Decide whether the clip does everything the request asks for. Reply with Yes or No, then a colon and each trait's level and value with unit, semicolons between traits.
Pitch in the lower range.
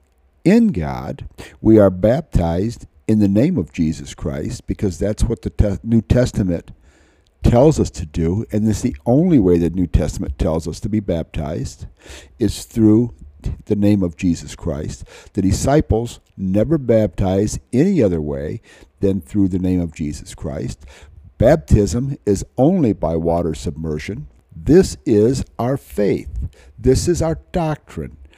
Yes: low, 100 Hz